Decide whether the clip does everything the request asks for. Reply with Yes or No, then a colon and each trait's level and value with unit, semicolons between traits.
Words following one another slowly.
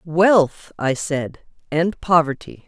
Yes: slow, 110 wpm